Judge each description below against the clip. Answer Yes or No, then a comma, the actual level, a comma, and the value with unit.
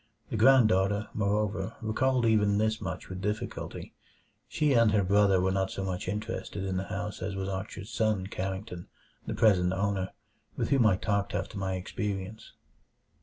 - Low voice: Yes, low, 100 Hz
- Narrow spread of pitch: Yes, narrow, 2.3 semitones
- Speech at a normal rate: Yes, average, 165 wpm